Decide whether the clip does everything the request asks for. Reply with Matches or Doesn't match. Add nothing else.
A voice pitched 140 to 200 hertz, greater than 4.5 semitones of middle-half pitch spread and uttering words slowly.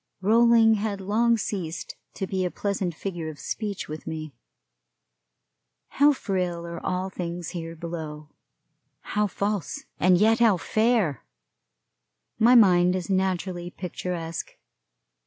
Doesn't match